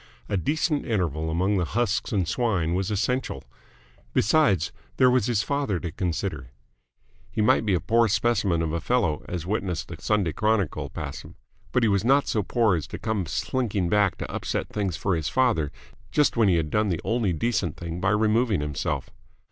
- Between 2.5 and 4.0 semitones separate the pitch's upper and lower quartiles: No, average, 5.0 semitones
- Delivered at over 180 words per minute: Yes, average, 190 wpm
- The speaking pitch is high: No, low, 100 Hz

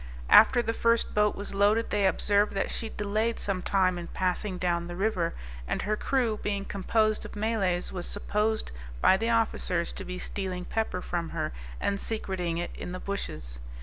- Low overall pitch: No, high, 200 Hz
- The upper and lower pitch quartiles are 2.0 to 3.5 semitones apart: Yes, average, 3.1 semitones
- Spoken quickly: No, average, 180 wpm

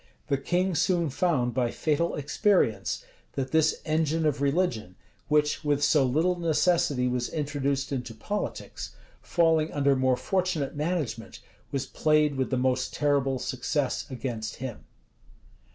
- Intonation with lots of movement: No, average, 3.6 semitones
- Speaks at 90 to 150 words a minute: Yes, slow, 135 wpm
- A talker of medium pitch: Yes, medium, 145 Hz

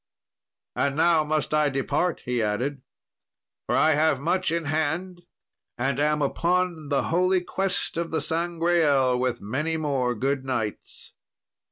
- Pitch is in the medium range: Yes, medium, 150 Hz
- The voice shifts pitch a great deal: No, average, 3.9 semitones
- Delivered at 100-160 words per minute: Yes, average, 140 wpm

